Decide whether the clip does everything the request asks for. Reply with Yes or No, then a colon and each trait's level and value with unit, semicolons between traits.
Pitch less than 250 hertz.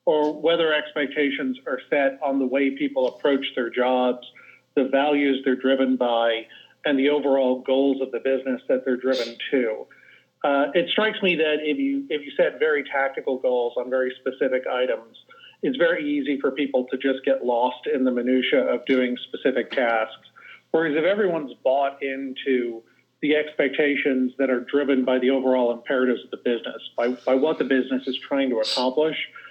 Yes: low, 135 Hz